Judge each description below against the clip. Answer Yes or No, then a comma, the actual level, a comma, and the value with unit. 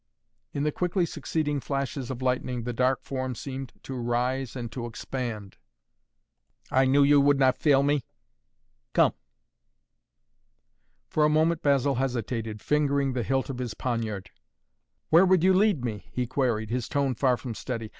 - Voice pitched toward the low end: Yes, low, 130 Hz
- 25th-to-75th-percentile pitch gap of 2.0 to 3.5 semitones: Yes, average, 2.9 semitones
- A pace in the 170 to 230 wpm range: No, average, 155 wpm